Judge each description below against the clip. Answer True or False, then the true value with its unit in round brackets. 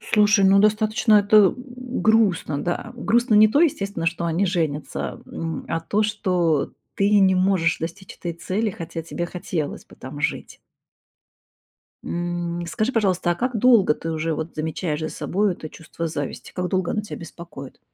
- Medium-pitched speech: True (180 Hz)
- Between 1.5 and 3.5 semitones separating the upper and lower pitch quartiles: False (4.3 semitones)